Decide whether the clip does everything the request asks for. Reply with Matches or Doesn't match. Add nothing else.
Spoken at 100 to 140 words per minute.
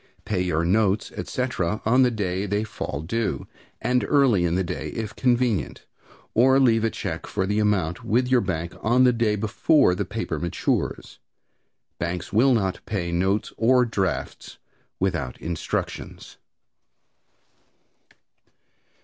Matches